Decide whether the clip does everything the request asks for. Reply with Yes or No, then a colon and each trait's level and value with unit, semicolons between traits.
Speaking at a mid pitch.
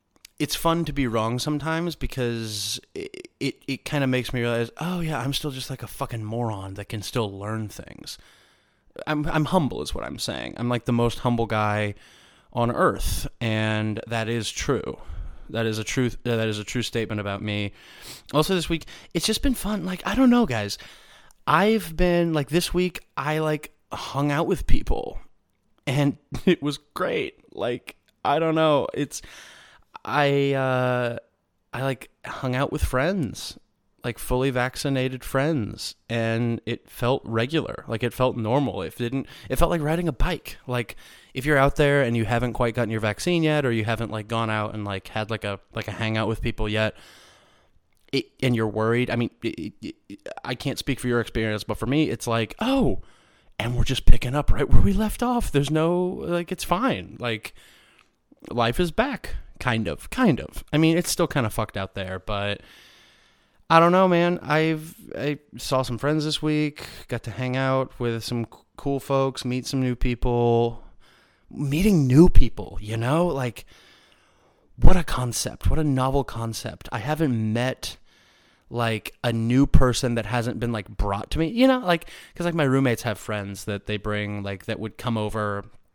No: low, 125 Hz